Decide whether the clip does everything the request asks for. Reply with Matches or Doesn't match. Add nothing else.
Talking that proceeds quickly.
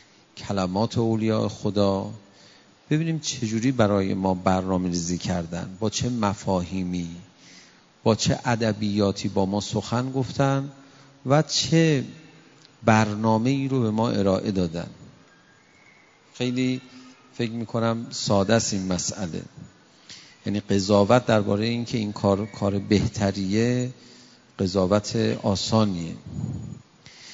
Doesn't match